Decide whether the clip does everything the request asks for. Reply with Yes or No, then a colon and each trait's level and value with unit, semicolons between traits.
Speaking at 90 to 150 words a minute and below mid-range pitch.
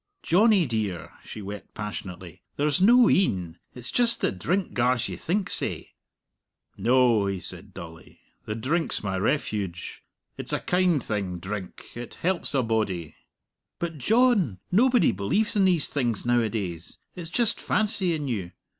Yes: average, 145 wpm; low, 120 Hz